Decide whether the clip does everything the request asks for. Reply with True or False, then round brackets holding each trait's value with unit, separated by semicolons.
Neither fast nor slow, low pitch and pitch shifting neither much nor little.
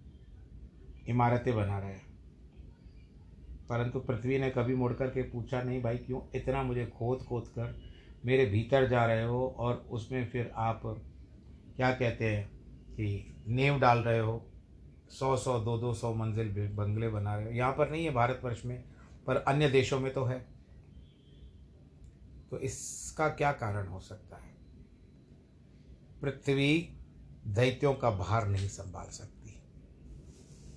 False (140 wpm; 115 Hz; 5.8 semitones)